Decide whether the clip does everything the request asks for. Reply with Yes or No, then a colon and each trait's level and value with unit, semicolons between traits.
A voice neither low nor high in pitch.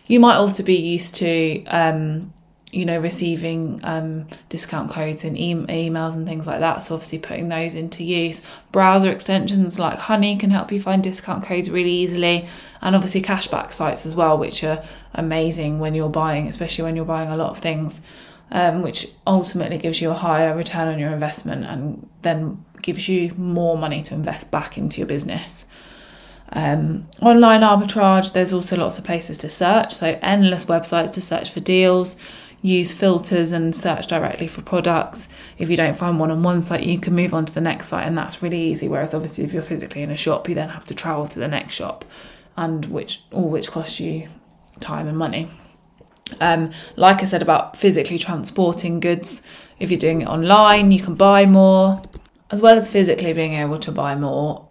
Yes: medium, 170 Hz